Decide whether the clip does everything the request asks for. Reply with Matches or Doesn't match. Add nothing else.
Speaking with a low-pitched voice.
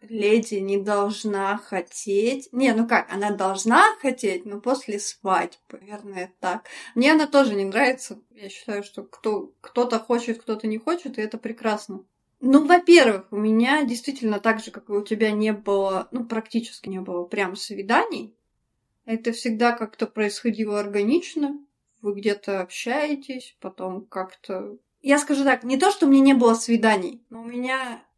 Doesn't match